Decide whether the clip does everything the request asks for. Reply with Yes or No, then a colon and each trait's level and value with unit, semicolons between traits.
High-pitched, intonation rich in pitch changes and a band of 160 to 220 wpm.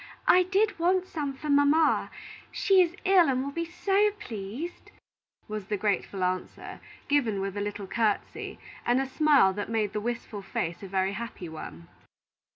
Yes: high, 240 Hz; wide, 8.4 semitones; average, 165 wpm